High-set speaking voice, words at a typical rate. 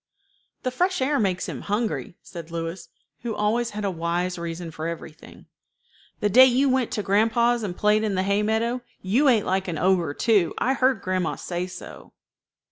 Yes: high, 205 Hz; average, 185 wpm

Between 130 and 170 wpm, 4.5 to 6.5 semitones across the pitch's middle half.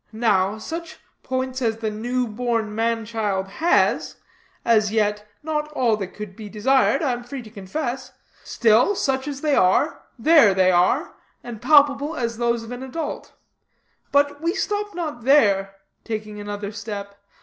Yes: average, 160 wpm; average, 5.0 semitones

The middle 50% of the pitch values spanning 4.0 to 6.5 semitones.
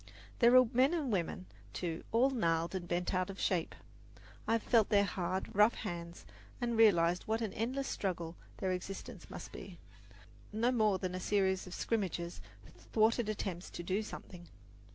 Yes: average, 4.3 semitones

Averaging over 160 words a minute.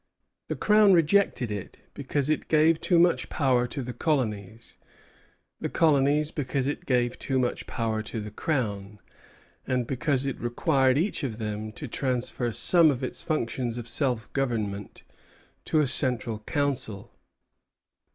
No: average, 145 wpm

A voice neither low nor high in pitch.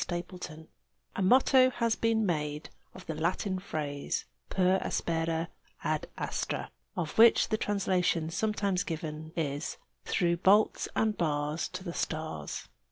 Yes: medium, 175 Hz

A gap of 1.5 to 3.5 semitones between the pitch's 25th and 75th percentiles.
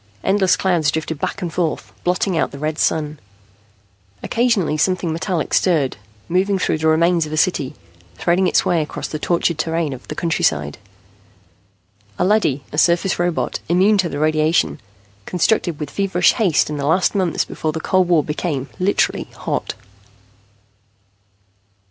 Yes: average, 3.0 semitones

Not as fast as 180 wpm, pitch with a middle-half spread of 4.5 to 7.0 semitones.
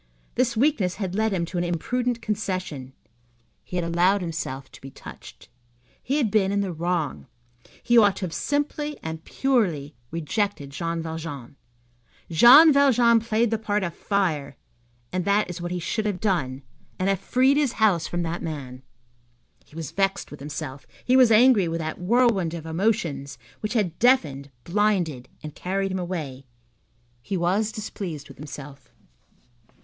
Yes: average, 165 wpm; average, 5.3 semitones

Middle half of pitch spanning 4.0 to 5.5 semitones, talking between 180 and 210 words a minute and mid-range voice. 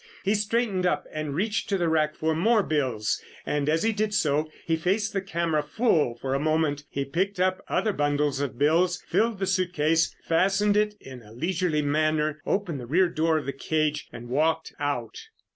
Yes: average, 4.5 semitones; average, 195 wpm; medium, 160 Hz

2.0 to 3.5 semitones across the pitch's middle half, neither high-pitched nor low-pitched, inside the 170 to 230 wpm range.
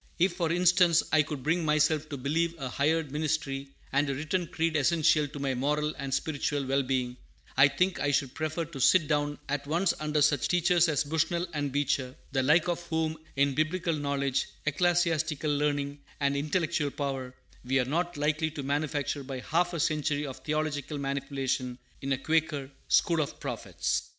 Yes: narrow, 2.5 semitones; medium, 150 Hz; average, 180 wpm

